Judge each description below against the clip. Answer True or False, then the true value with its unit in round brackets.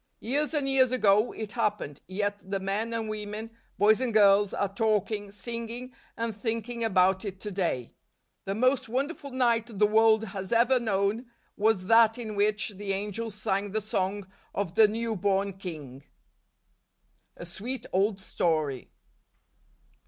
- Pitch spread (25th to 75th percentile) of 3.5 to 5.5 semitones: False (2.7 semitones)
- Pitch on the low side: False (210 Hz)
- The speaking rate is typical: True (150 wpm)